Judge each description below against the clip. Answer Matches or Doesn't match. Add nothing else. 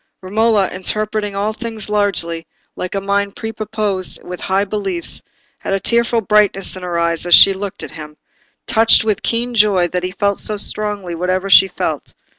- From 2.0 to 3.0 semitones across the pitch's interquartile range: Matches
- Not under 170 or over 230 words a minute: Matches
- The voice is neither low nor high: Doesn't match